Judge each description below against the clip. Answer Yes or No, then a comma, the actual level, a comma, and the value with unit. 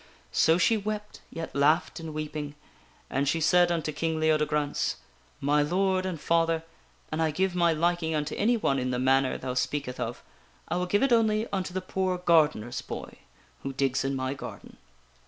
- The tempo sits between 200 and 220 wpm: No, average, 185 wpm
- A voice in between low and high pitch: Yes, medium, 160 Hz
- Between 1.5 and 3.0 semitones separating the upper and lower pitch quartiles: No, average, 4.0 semitones